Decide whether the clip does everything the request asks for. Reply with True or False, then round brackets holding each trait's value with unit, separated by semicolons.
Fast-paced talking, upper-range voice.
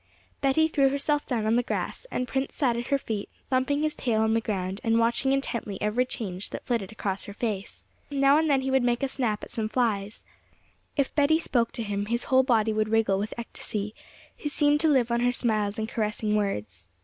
True (220 wpm; 235 Hz)